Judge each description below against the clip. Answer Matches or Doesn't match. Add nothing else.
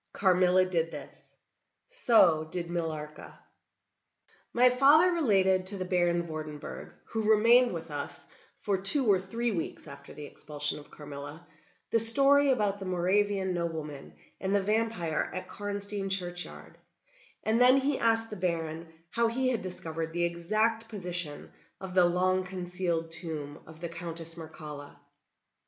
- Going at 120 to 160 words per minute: Matches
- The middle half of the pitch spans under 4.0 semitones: Doesn't match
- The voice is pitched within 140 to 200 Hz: Matches